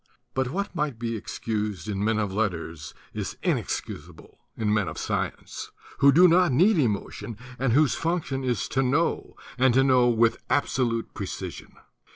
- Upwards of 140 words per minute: Yes, average, 170 wpm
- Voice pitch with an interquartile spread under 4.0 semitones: No, average, 4.7 semitones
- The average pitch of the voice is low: Yes, low, 125 Hz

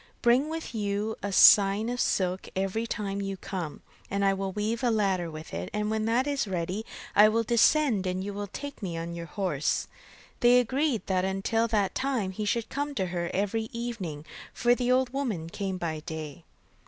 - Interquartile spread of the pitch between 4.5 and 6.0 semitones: No, average, 4.0 semitones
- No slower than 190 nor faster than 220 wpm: Yes, average, 200 wpm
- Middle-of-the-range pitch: No, high, 205 Hz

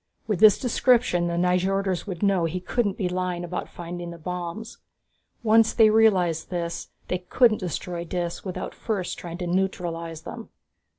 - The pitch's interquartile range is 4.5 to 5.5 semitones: No, average, 2.8 semitones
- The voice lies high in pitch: No, medium, 180 Hz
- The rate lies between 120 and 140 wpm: No, average, 160 wpm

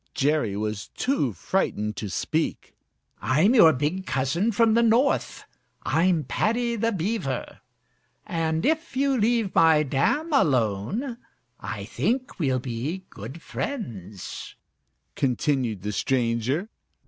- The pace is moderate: No, slow, 115 wpm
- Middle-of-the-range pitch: Yes, medium, 160 Hz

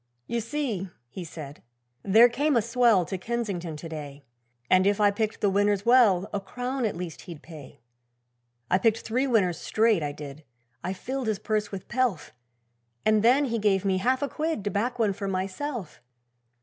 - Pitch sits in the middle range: No, high, 205 Hz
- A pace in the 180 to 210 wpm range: Yes, average, 185 wpm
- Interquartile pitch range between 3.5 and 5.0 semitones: Yes, average, 4.4 semitones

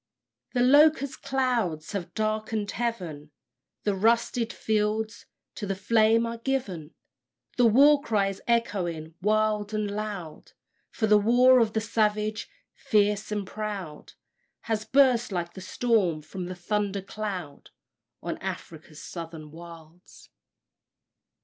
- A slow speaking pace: Yes, slow, 125 wpm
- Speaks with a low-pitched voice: No, high, 210 Hz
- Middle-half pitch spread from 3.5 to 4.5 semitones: Yes, average, 4.1 semitones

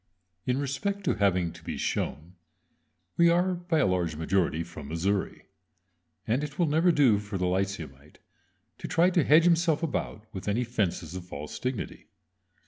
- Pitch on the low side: Yes, low, 105 Hz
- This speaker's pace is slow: No, average, 165 wpm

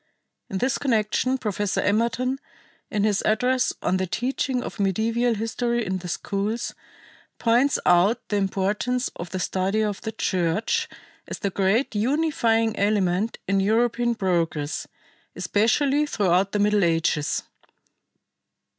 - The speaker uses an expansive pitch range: No, average, 3.8 semitones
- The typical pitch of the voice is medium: No, high, 210 Hz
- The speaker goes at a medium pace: No, slow, 130 wpm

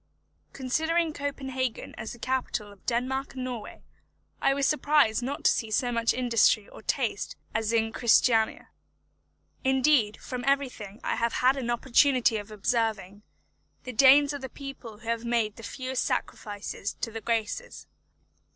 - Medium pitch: No, high, 245 Hz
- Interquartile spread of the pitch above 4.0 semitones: No, average, 3.1 semitones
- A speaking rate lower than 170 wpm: Yes, average, 150 wpm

